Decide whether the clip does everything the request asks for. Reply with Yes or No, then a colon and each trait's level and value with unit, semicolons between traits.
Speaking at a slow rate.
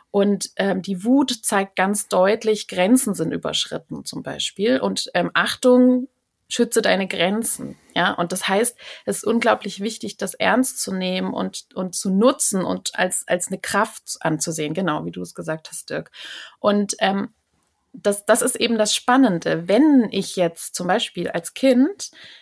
No: average, 165 wpm